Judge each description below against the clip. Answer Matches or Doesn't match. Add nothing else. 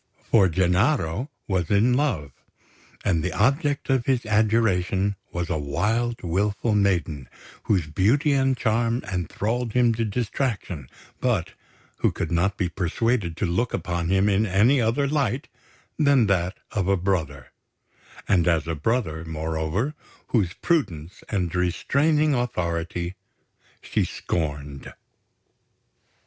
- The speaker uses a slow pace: Matches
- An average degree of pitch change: Doesn't match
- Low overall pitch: Matches